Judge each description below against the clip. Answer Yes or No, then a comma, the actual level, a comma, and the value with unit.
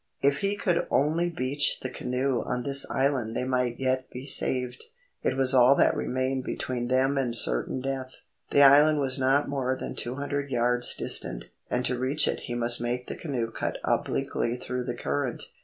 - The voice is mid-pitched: No, low, 130 Hz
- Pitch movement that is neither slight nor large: No, narrow, 2.0 semitones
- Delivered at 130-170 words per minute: No, average, 190 wpm